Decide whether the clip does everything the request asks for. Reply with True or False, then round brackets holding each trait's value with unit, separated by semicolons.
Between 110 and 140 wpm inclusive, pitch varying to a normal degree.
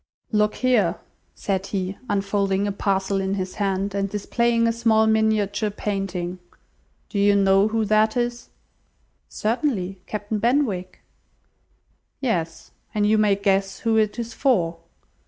False (135 wpm; 2.1 semitones)